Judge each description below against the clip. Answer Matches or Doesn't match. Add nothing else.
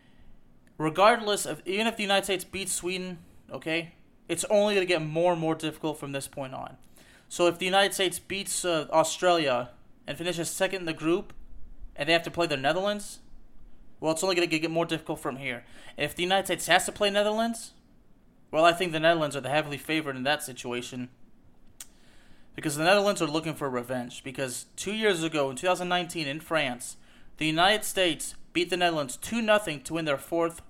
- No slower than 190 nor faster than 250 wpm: Matches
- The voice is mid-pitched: Matches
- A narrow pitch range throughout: Doesn't match